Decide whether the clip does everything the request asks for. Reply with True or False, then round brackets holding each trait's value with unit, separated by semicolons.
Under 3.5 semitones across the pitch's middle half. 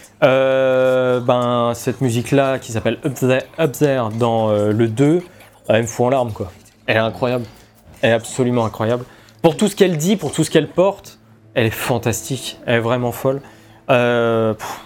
True (3.0 semitones)